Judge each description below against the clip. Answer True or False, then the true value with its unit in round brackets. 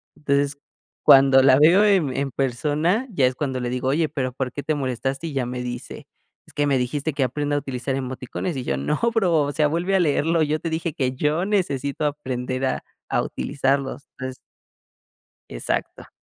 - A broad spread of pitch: False (3.0 semitones)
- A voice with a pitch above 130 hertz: True (140 Hz)